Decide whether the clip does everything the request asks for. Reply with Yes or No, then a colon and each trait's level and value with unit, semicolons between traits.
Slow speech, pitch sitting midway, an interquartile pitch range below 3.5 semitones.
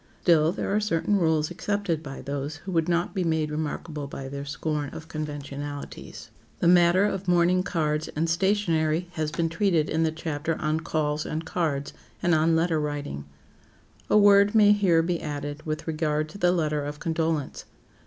No: average, 175 wpm; medium, 160 Hz; narrow, 2.6 semitones